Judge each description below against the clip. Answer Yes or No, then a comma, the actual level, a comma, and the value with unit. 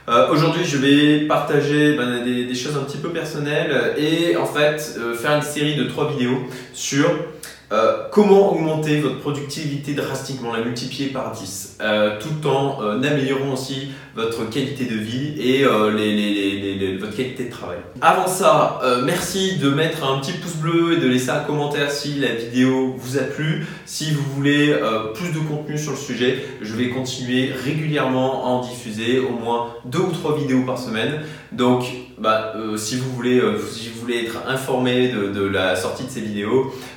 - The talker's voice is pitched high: No, low, 130 Hz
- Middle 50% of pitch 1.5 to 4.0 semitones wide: Yes, average, 3.5 semitones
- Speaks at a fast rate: No, average, 195 wpm